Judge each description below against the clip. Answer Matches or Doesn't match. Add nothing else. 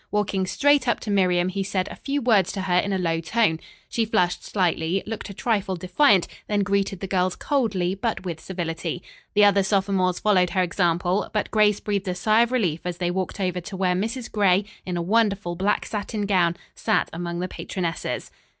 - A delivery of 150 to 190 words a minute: Doesn't match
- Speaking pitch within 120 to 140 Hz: Doesn't match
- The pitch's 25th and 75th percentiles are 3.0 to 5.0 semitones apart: Doesn't match